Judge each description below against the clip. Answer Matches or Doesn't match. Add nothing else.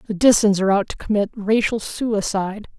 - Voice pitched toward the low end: Doesn't match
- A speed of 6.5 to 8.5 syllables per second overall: Doesn't match